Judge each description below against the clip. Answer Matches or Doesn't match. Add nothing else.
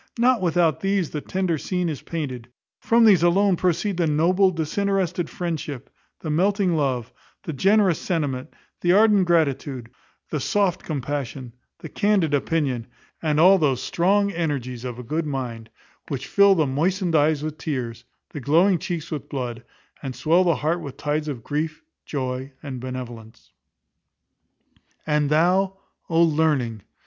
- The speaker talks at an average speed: Matches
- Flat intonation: Doesn't match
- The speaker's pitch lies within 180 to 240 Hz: Doesn't match